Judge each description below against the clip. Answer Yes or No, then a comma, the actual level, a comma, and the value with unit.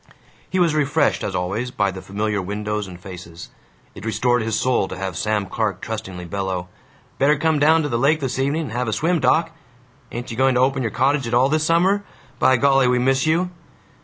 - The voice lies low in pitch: Yes, low, 125 Hz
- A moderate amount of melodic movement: No, wide, 6.2 semitones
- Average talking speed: No, fast, 215 wpm